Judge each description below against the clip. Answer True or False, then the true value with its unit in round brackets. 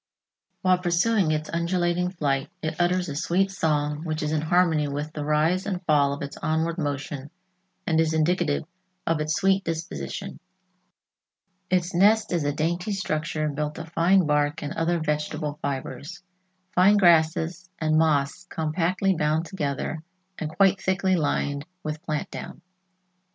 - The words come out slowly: False (150 wpm)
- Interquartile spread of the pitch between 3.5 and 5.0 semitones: False (3.0 semitones)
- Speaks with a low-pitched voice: False (160 Hz)